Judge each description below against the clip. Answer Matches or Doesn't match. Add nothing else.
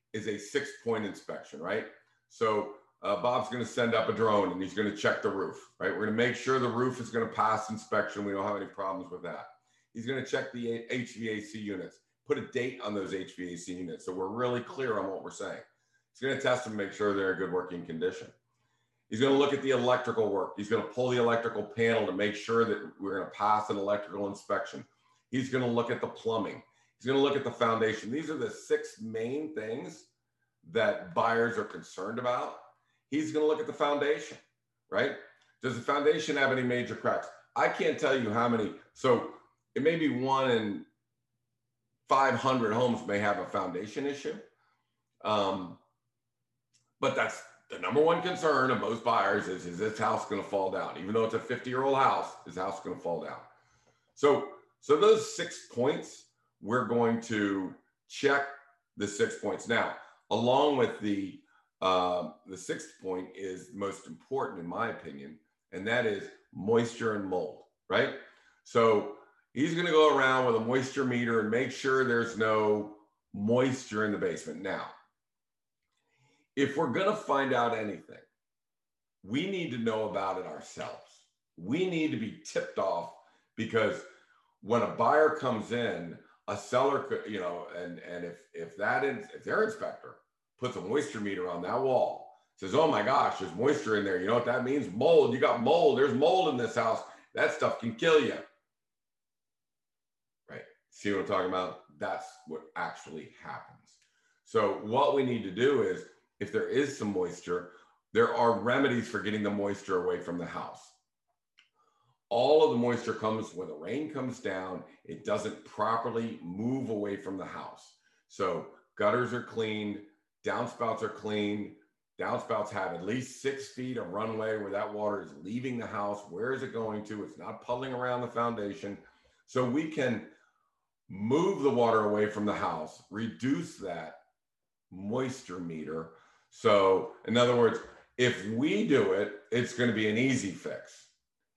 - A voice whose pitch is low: Matches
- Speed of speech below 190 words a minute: Matches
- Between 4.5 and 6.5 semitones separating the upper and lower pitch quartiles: Doesn't match